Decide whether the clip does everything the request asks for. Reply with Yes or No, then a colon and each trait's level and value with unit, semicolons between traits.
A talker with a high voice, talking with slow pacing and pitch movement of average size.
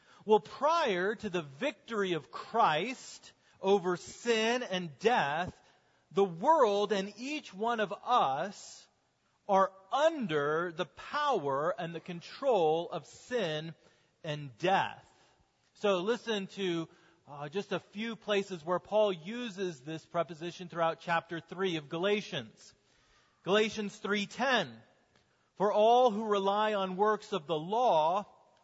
Yes: high, 195 Hz; slow, 120 wpm; average, 4.3 semitones